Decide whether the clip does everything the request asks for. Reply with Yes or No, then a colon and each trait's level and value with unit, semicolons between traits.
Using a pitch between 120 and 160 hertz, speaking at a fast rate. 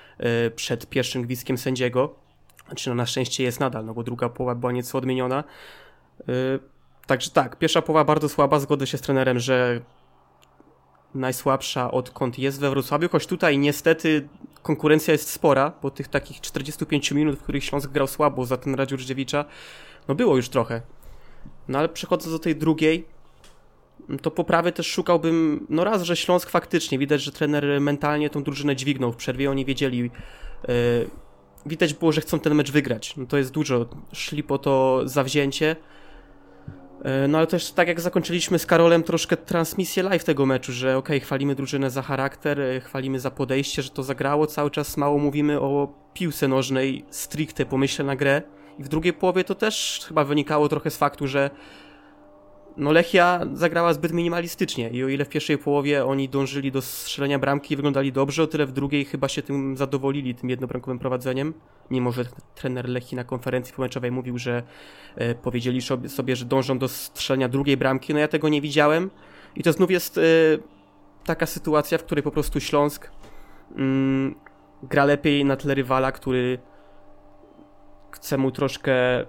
Yes: medium, 140 Hz; fast, 165 wpm